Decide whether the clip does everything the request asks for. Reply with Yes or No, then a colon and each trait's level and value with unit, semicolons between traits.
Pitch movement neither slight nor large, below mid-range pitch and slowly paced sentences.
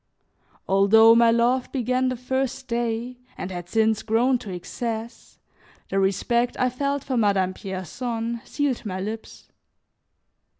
No: average, 3.6 semitones; high, 230 Hz; slow, 130 wpm